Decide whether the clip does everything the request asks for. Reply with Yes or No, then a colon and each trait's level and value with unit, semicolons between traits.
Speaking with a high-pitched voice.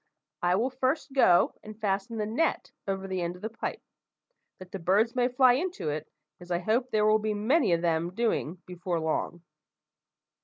Yes: high, 210 Hz